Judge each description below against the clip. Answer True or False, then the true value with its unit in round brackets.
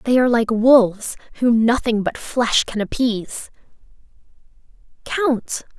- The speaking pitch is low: False (235 Hz)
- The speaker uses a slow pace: True (115 wpm)